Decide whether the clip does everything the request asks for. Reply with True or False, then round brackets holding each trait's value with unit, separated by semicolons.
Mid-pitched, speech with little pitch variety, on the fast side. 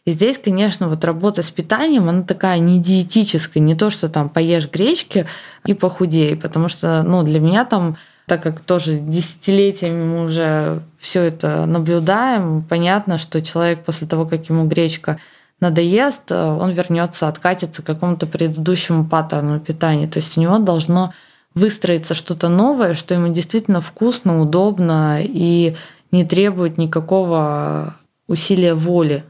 False (170 Hz; 2.2 semitones; 145 wpm)